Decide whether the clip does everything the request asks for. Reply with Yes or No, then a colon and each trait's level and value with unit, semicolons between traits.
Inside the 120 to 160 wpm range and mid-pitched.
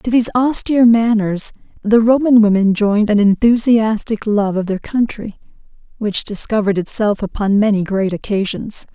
No: average, 140 wpm; high, 215 Hz